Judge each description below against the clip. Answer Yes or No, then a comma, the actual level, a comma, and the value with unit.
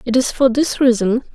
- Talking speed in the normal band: No, fast, 220 wpm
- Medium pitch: No, high, 245 Hz